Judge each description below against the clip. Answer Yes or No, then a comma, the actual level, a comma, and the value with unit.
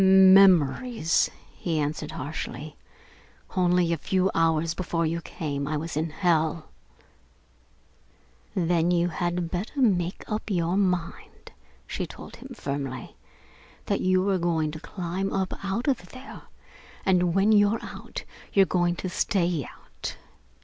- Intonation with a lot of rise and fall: No, average, 2.8 semitones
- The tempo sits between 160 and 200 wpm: No, slow, 135 wpm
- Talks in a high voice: No, medium, 175 Hz